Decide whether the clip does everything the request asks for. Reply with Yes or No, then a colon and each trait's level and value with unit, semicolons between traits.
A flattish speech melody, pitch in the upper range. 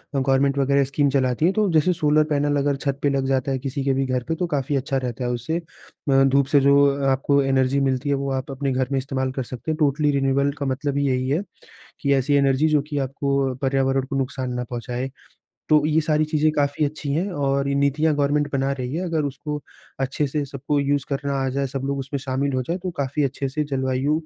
No: narrow, 1.6 semitones; medium, 140 Hz